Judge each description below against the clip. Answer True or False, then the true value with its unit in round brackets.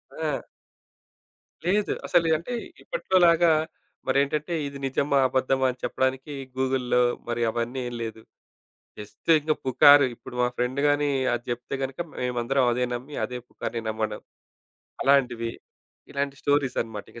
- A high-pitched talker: False (130 Hz)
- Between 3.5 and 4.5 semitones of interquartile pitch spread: False (3.0 semitones)